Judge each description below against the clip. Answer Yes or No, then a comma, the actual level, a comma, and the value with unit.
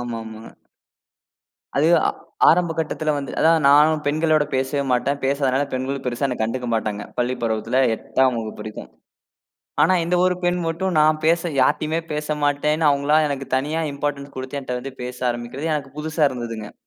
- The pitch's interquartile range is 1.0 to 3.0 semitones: No, average, 3.6 semitones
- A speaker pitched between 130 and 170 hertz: Yes, medium, 140 Hz